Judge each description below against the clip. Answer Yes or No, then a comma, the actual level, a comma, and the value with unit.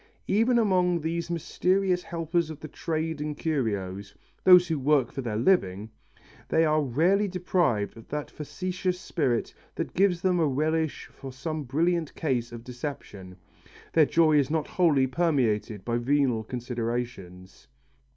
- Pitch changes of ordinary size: No, wide, 6.0 semitones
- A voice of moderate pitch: Yes, medium, 150 Hz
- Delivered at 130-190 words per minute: Yes, average, 145 wpm